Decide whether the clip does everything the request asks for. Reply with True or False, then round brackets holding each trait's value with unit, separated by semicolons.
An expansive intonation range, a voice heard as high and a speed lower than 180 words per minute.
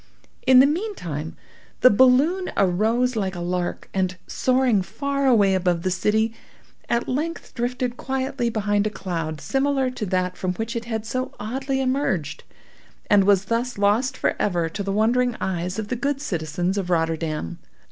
True (5.8 semitones; 220 Hz; 160 wpm)